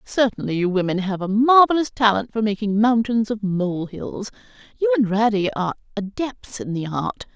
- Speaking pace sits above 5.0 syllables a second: Yes, 5.2 syllables/s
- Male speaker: No, female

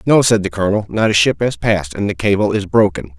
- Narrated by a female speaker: No, male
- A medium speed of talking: No, fast, 265 wpm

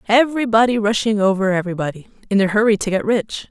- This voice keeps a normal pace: Yes, average, 170 wpm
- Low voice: No, high, 210 Hz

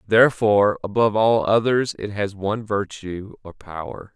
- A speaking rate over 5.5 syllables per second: No, 4.9 syllables/s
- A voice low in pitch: Yes, low, 105 Hz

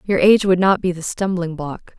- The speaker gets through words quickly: Yes, fast, 240 wpm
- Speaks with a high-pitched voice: No, medium, 180 Hz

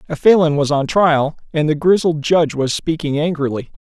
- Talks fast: No, average, 185 wpm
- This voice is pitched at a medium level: Yes, medium, 155 Hz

